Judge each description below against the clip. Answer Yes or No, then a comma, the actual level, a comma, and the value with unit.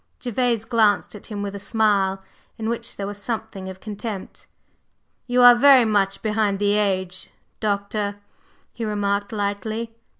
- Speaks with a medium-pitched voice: No, high, 210 Hz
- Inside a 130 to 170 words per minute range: Yes, average, 145 wpm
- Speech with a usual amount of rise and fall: No, narrow, 2.0 semitones